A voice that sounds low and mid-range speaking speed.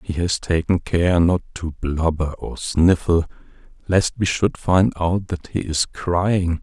Yes: very low, 85 Hz; average, 165 wpm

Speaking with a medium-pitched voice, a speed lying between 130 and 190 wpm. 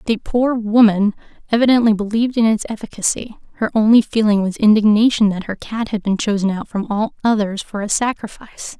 No: high, 215 Hz; average, 175 wpm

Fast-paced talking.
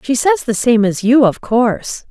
Yes: fast, 230 wpm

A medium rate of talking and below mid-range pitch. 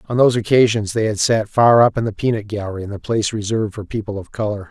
No: fast, 255 wpm; low, 110 Hz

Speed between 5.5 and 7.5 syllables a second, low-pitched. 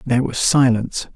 Yes: 6.1 syllables/s; low, 125 Hz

